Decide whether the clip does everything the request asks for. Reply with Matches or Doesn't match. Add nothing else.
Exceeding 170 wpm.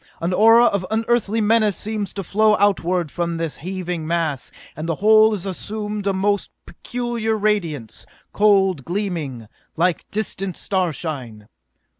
Doesn't match